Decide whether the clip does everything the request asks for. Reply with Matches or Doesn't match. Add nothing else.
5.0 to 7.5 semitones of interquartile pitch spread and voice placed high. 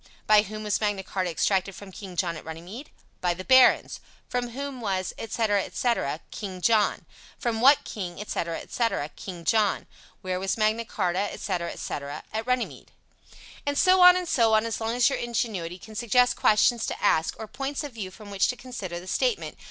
Doesn't match